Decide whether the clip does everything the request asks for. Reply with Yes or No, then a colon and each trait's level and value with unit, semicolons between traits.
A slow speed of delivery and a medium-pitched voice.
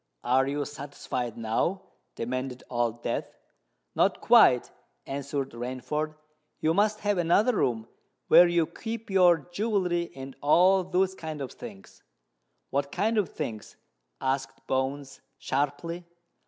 Yes: slow, 125 wpm; medium, 145 Hz